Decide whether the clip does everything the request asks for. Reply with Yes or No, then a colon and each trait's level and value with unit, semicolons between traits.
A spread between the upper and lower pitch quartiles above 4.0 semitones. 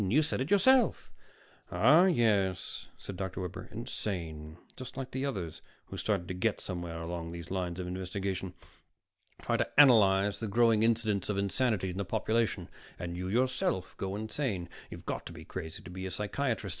Yes: average, 4.4 semitones